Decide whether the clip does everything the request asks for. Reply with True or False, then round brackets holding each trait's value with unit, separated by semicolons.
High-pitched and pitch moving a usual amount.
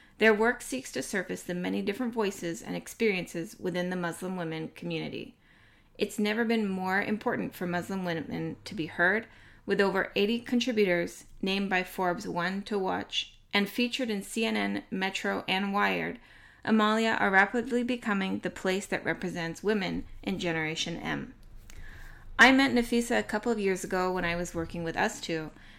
True (195 Hz; 4.0 semitones)